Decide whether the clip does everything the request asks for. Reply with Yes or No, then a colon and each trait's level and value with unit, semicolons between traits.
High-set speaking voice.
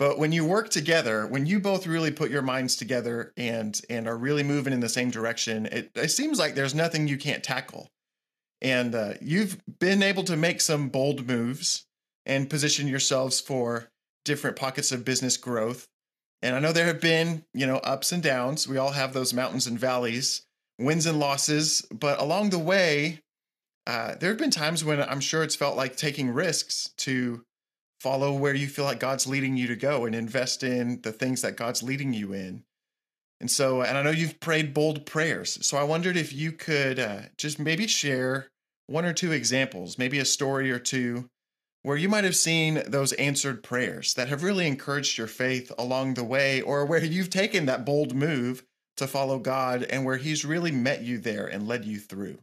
No: low, 135 Hz